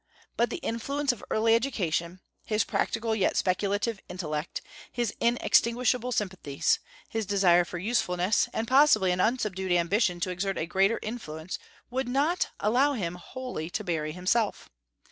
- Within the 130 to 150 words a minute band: Yes, average, 145 wpm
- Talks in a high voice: Yes, high, 205 Hz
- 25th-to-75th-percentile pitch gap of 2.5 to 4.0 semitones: No, average, 4.9 semitones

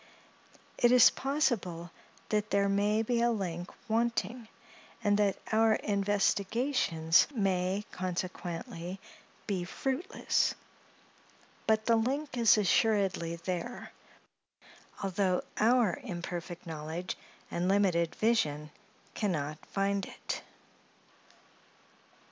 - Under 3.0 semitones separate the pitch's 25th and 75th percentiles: No, average, 4.2 semitones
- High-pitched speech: Yes, high, 200 Hz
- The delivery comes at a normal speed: No, slow, 95 wpm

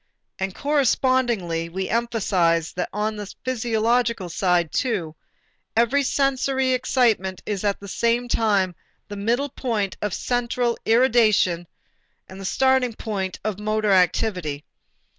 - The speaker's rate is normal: No, slow, 120 wpm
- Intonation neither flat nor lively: Yes, average, 4.4 semitones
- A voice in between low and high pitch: No, high, 215 Hz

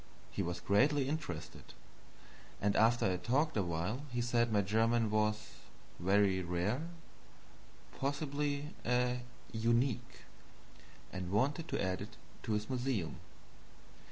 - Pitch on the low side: Yes, low, 115 Hz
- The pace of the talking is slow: Yes, slow, 125 wpm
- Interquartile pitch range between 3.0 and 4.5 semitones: No, average, 5.0 semitones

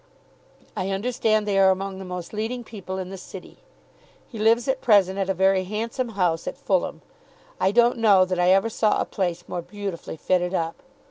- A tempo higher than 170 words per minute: Yes, average, 195 wpm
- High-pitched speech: Yes, high, 195 Hz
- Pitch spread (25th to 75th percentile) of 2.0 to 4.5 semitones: Yes, average, 3.0 semitones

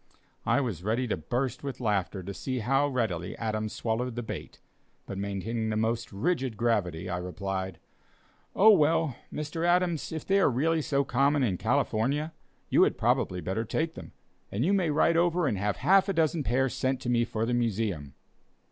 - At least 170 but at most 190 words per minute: Yes, average, 185 wpm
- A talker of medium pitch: No, low, 120 Hz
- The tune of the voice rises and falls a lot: Yes, wide, 6.2 semitones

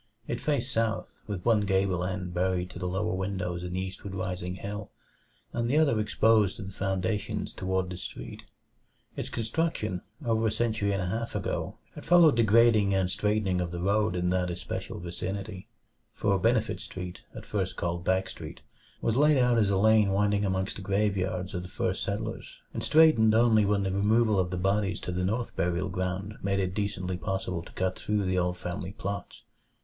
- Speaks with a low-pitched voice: Yes, low, 100 Hz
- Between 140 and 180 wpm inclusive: No, average, 195 wpm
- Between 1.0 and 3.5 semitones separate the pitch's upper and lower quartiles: Yes, average, 2.9 semitones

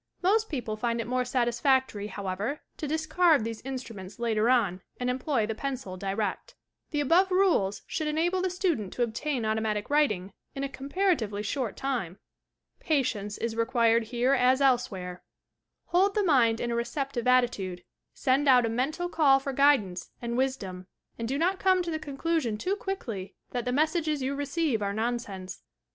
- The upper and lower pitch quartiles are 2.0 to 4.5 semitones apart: No, wide, 5.4 semitones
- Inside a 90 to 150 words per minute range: No, average, 170 wpm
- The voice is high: Yes, very high, 250 Hz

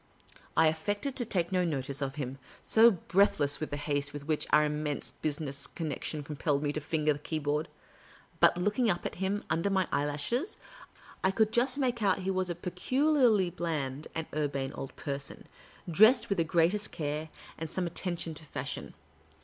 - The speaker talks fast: No, average, 185 wpm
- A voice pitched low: No, medium, 160 Hz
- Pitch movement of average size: Yes, average, 4.8 semitones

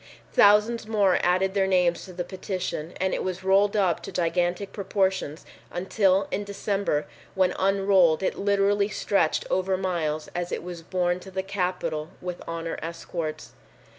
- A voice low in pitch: No, medium, 185 Hz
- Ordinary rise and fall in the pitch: No, narrow, 2.1 semitones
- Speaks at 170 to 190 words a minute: No, average, 155 wpm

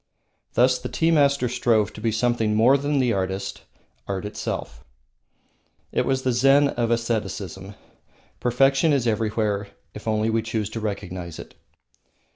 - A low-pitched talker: Yes, low, 115 Hz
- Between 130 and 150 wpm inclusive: Yes, average, 145 wpm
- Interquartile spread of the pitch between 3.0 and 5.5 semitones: Yes, average, 3.4 semitones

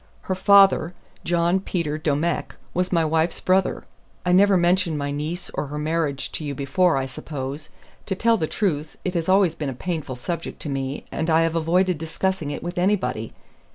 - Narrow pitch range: No, average, 3.7 semitones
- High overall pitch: No, medium, 165 Hz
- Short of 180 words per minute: No, average, 190 wpm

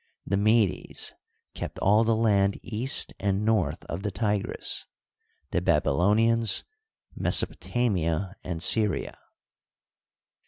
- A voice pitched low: Yes, low, 105 Hz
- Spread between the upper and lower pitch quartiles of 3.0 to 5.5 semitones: No, narrow, 2.5 semitones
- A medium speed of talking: No, slow, 105 wpm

